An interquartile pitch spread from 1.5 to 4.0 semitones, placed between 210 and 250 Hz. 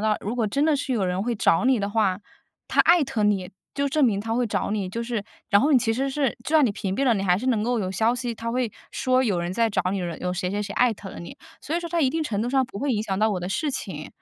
No: average, 4.5 semitones; high, 225 Hz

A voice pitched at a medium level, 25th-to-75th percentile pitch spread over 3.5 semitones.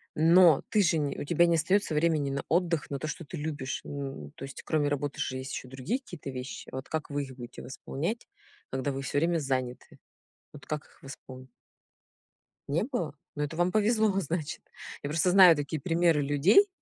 Yes: medium, 150 Hz; average, 4.0 semitones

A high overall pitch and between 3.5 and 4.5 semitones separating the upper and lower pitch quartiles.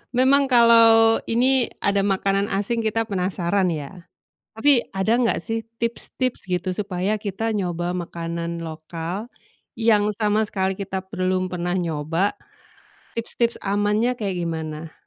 Yes: high, 200 Hz; average, 4.2 semitones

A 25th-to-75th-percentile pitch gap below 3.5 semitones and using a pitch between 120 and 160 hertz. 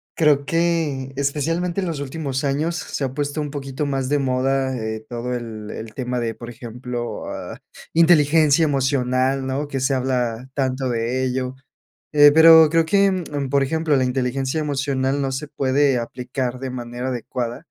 Yes: average, 2.7 semitones; low, 135 Hz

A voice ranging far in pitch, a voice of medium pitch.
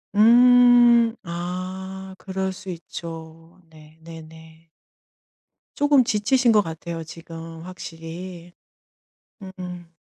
No: average, 4.0 semitones; medium, 180 Hz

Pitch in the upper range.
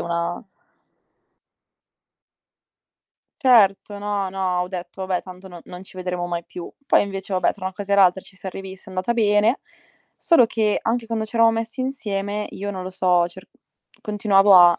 Yes: high, 195 Hz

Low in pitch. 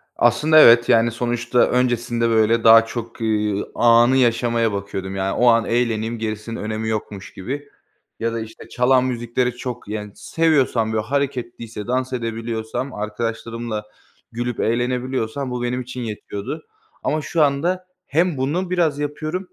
Yes: low, 120 Hz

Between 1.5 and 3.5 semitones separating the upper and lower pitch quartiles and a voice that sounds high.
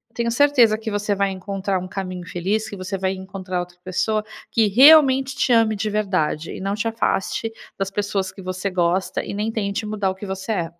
Yes: average, 2.7 semitones; high, 200 Hz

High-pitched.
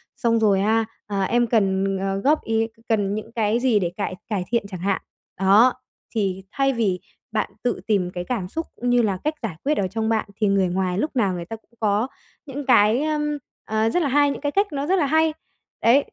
Yes: high, 220 Hz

